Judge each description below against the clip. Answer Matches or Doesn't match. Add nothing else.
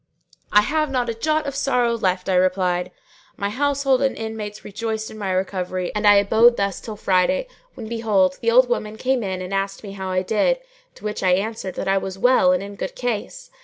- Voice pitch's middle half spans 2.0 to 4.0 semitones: Doesn't match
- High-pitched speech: Matches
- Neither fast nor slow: Doesn't match